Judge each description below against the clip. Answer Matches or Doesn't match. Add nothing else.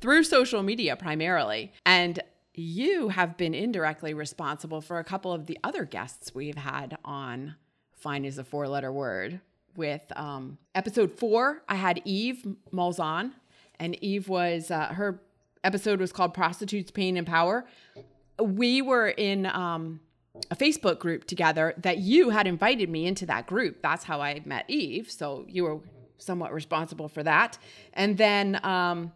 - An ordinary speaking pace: Matches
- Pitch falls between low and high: Matches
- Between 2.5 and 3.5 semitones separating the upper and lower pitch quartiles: Doesn't match